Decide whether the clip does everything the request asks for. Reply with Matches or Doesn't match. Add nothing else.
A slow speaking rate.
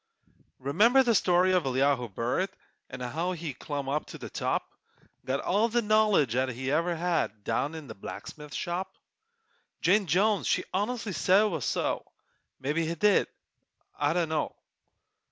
Doesn't match